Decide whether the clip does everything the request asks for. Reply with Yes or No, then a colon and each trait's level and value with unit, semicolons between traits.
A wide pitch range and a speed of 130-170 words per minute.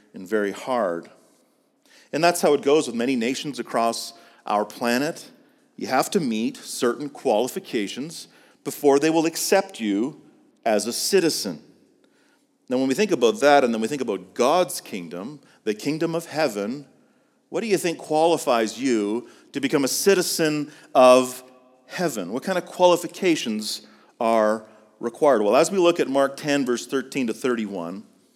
Yes: wide, 6.2 semitones; average, 155 wpm